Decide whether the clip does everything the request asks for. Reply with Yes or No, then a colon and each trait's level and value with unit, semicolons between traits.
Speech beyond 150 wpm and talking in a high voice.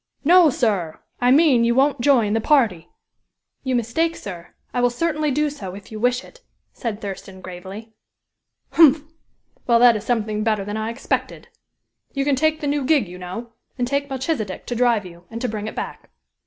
Yes: average, 190 wpm; high, 235 Hz